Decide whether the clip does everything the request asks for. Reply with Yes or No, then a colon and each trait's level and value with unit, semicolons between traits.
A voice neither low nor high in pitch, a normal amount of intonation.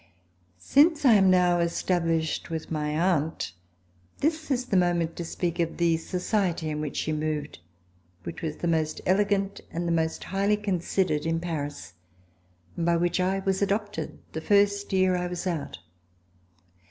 Yes: medium, 175 Hz; average, 3.2 semitones